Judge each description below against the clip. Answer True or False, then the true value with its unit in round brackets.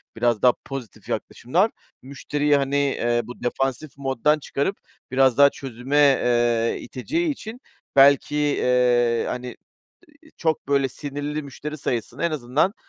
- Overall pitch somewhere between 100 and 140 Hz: True (135 Hz)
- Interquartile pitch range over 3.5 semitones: False (3.1 semitones)